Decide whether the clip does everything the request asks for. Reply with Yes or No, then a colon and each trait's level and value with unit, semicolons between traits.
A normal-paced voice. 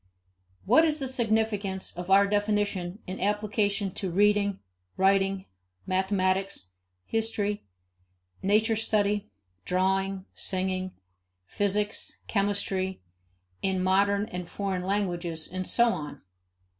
No: slow, 95 wpm